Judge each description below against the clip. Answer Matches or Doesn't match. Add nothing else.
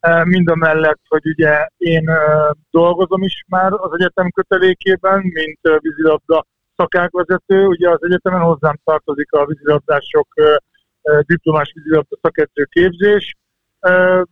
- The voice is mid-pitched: Matches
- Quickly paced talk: Doesn't match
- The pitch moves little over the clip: Doesn't match